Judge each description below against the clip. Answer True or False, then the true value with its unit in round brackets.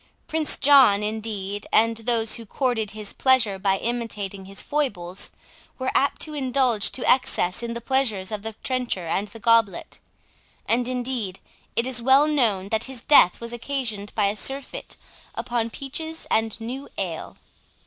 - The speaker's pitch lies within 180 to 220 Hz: False (230 Hz)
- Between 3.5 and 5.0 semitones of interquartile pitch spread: True (4.2 semitones)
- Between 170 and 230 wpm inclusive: False (160 wpm)